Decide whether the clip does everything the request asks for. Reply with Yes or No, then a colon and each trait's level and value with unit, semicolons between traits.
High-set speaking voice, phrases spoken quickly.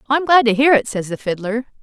Yes: high, 245 Hz; fast, 295 wpm